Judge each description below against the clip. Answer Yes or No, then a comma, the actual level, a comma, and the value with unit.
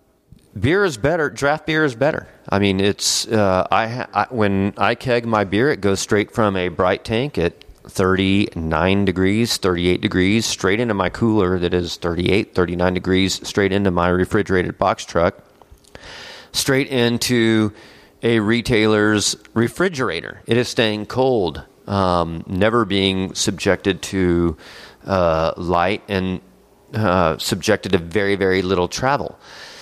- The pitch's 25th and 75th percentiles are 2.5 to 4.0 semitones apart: Yes, average, 3.3 semitones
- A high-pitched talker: No, low, 100 Hz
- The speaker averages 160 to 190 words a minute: No, average, 145 wpm